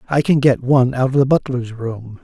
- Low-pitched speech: Yes, low, 130 Hz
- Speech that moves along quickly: Yes, fast, 240 wpm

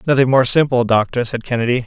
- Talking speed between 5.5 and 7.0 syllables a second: Yes, 6.4 syllables/s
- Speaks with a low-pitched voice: Yes, low, 125 Hz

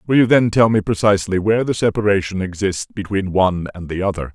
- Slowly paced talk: No, fast, 205 wpm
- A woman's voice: No, male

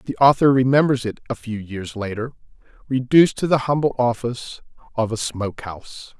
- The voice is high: No, low, 125 Hz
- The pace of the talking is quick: No, average, 165 wpm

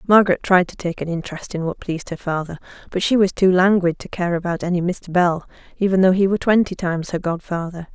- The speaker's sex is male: No, female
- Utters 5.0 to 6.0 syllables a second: No, 6.3 syllables/s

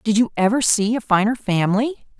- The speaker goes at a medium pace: Yes, average, 190 wpm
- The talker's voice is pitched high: Yes, high, 220 Hz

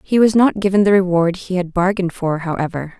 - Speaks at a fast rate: Yes, fast, 220 wpm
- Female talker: Yes, female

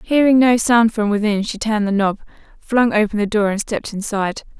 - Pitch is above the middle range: Yes, high, 215 Hz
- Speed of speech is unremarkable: No, fast, 210 wpm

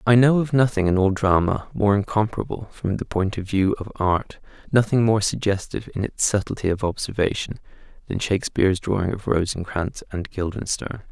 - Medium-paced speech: Yes, average, 165 wpm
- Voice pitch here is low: Yes, low, 100 Hz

